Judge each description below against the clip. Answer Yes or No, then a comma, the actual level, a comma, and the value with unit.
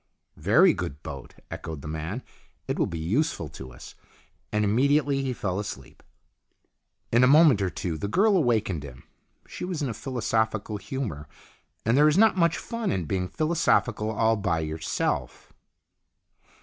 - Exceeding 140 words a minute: Yes, average, 165 wpm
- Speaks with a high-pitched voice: No, low, 110 Hz